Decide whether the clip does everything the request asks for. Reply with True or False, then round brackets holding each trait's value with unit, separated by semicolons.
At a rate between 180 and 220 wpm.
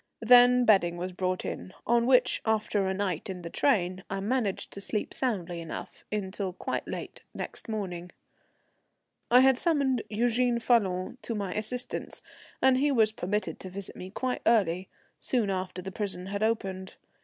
False (165 wpm)